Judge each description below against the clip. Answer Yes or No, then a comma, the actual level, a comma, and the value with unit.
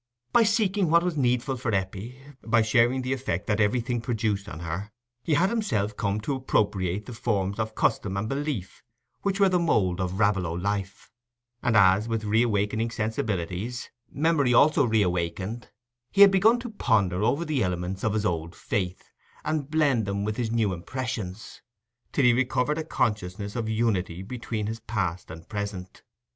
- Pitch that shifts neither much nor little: Yes, average, 4.7 semitones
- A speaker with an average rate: Yes, average, 170 wpm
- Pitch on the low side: Yes, low, 110 Hz